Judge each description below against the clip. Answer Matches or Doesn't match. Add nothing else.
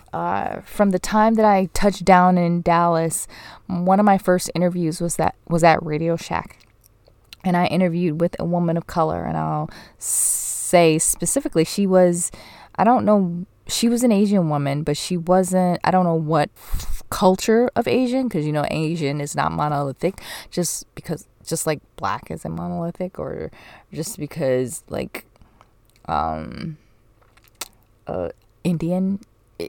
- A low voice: Doesn't match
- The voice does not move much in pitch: Doesn't match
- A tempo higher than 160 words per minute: Doesn't match